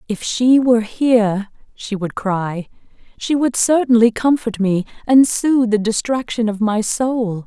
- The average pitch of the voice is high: Yes, high, 225 Hz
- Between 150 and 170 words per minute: Yes, average, 155 wpm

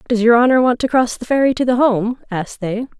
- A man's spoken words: No, female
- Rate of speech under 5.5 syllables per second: No, 6.4 syllables/s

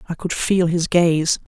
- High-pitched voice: No, medium, 170 Hz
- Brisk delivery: No, average, 195 wpm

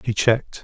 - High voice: No, low, 115 Hz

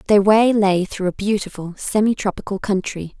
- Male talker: No, female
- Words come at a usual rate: Yes, average, 170 wpm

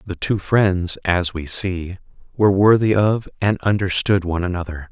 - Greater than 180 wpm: No, average, 160 wpm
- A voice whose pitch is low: Yes, very low, 95 Hz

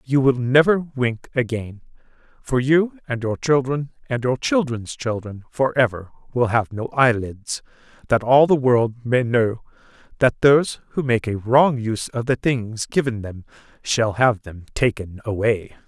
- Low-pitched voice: Yes, low, 120 Hz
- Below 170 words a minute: Yes, average, 160 wpm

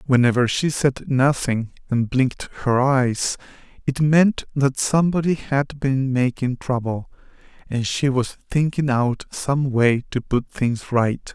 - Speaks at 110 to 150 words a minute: Yes, average, 145 wpm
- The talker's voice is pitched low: Yes, low, 130 Hz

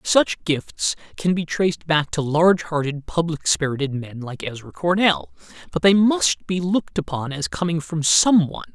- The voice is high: No, medium, 160 Hz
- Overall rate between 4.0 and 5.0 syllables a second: Yes, 4.8 syllables/s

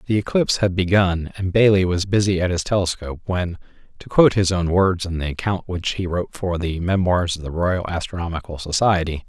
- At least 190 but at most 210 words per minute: Yes, average, 200 wpm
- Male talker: Yes, male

